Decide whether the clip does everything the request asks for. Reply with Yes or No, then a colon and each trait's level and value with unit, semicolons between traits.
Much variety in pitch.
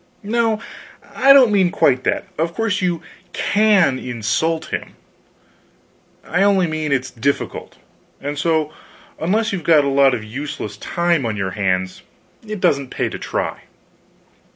Yes: wide, 7.0 semitones